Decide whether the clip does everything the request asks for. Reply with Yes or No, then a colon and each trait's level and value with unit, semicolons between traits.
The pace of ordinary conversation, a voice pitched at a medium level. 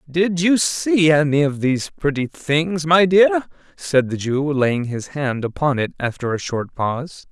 Yes: average, 180 wpm; medium, 150 Hz